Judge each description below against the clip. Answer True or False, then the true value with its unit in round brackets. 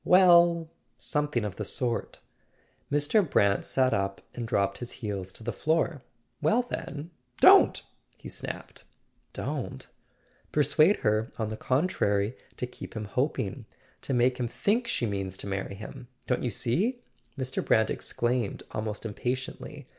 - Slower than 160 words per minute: True (145 wpm)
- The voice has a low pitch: True (125 Hz)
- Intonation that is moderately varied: False (6.0 semitones)